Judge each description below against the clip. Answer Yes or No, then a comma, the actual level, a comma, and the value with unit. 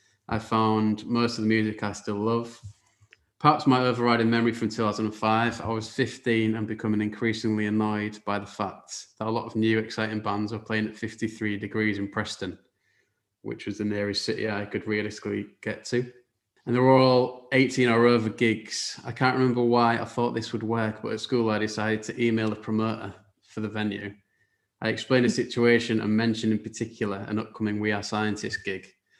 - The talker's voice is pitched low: Yes, low, 110 Hz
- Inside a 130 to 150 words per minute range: No, average, 190 wpm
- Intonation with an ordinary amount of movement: No, narrow, 1.7 semitones